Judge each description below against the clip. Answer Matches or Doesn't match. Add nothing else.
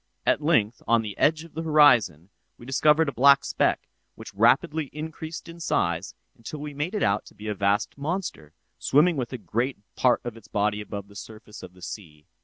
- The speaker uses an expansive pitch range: Matches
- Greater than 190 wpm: Matches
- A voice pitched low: Matches